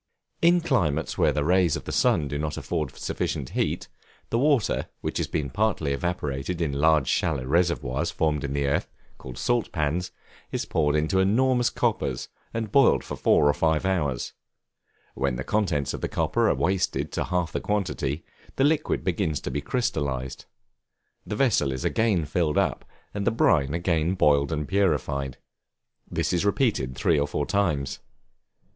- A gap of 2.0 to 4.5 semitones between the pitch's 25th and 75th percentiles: No, wide, 5.6 semitones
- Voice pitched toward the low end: Yes, very low, 80 Hz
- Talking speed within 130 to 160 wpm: No, average, 170 wpm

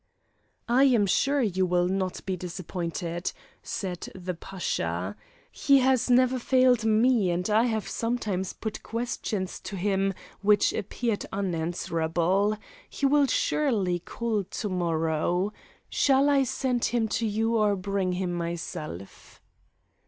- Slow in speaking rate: Yes, slow, 130 wpm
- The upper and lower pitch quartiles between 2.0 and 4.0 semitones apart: No, average, 4.8 semitones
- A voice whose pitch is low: No, high, 200 Hz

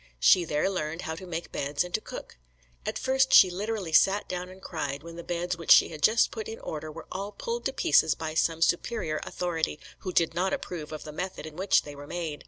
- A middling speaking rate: No, fast, 235 wpm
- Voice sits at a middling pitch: Yes, medium, 170 Hz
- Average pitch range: Yes, average, 3.4 semitones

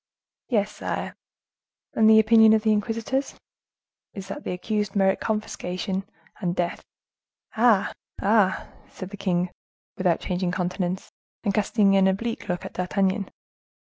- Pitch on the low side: No, high, 195 Hz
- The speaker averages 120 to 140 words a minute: Yes, slow, 135 wpm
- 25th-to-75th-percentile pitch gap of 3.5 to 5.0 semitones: No, average, 2.8 semitones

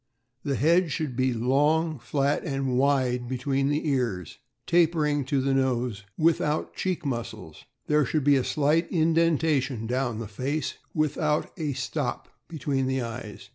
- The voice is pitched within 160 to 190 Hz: No, medium, 140 Hz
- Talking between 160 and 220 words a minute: No, average, 150 wpm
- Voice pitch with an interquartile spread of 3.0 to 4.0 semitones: Yes, average, 3.5 semitones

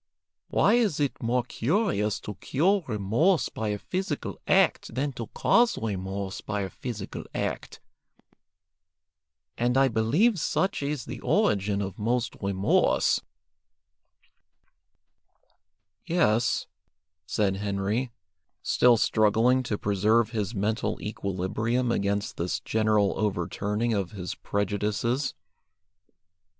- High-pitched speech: No, low, 110 Hz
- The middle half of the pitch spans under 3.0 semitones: No, average, 4.0 semitones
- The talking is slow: Yes, slow, 105 wpm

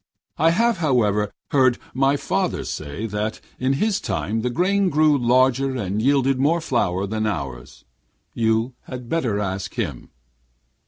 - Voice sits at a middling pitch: No, low, 125 Hz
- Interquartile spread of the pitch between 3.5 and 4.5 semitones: No, average, 5.2 semitones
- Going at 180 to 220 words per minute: No, average, 145 wpm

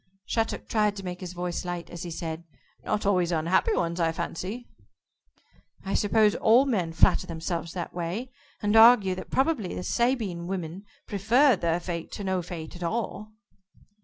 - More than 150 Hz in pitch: Yes, medium, 185 Hz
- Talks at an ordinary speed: Yes, average, 165 wpm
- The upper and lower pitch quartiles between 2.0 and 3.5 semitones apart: No, average, 4.0 semitones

